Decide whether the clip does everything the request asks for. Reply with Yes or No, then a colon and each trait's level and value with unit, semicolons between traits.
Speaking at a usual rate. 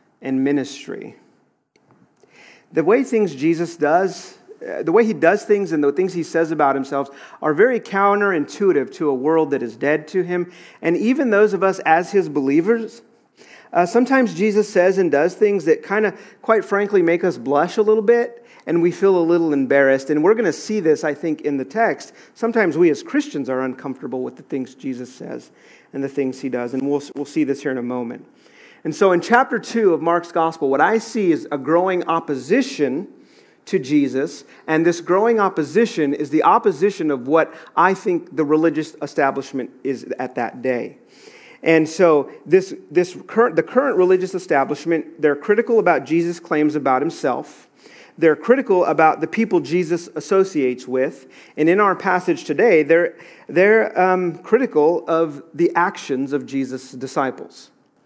Yes: average, 180 wpm